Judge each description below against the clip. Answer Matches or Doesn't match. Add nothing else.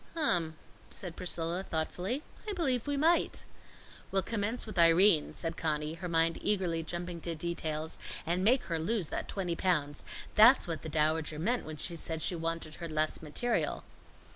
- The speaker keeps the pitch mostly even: Doesn't match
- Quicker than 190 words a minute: Doesn't match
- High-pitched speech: Doesn't match